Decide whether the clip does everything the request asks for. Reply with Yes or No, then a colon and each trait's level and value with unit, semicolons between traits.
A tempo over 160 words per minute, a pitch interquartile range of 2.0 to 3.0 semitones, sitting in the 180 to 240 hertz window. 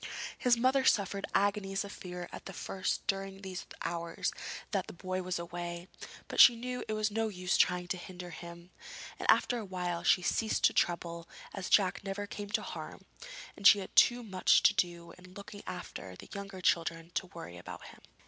Yes: average, 190 wpm; narrow, 2.6 semitones; medium, 185 Hz